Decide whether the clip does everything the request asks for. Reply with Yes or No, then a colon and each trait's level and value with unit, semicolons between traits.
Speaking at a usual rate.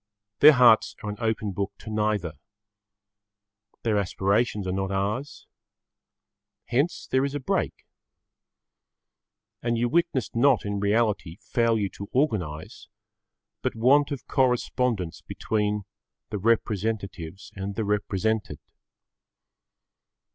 No: slow, 110 wpm